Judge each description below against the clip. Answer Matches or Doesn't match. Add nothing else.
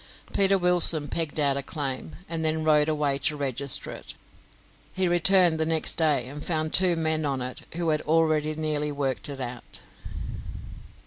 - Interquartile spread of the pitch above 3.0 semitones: Doesn't match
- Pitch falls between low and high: Matches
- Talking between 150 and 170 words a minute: Matches